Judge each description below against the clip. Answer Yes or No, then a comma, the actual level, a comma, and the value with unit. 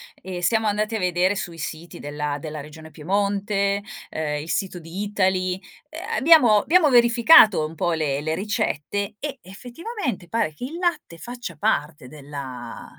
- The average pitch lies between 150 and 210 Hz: Yes, high, 190 Hz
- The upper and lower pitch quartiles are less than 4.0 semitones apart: No, wide, 6.1 semitones